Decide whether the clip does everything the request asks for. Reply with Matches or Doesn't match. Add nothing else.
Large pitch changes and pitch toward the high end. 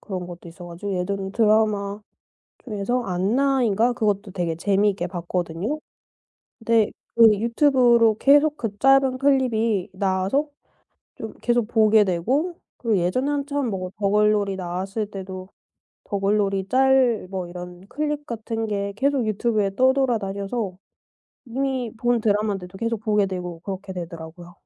Doesn't match